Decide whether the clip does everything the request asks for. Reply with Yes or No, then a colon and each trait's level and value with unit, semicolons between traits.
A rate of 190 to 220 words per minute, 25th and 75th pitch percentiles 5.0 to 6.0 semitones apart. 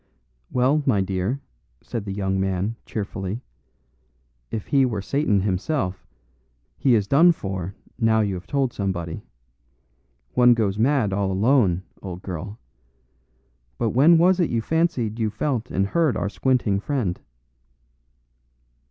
No: slow, 135 wpm; wide, 5.4 semitones